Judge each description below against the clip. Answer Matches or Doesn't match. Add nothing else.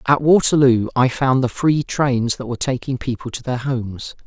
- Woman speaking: Doesn't match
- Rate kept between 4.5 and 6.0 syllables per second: Matches